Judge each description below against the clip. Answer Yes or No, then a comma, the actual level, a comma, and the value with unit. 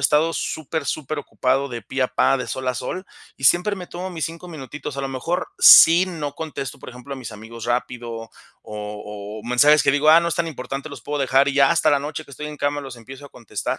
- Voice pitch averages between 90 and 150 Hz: Yes, medium, 140 Hz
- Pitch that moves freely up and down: No, average, 3.9 semitones